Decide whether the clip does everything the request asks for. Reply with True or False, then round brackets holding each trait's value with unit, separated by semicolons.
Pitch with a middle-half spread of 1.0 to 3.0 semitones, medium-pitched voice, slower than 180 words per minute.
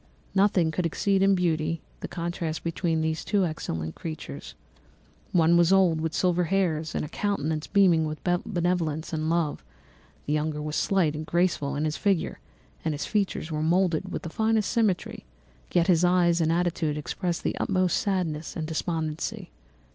True (2.7 semitones; 170 Hz; 165 wpm)